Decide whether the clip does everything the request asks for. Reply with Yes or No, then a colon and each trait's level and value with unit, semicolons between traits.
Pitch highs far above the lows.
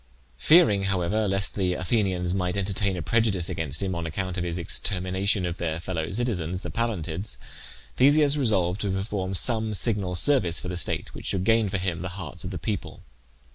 No: average, 3.0 semitones